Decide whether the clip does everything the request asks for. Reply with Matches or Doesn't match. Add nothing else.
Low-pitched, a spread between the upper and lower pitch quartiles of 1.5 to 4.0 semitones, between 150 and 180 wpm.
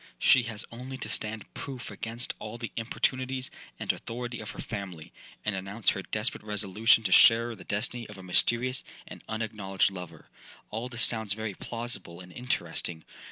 Matches